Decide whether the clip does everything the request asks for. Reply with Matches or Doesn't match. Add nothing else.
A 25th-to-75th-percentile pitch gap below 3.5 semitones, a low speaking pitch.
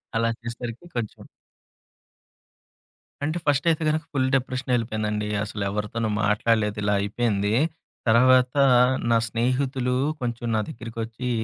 Matches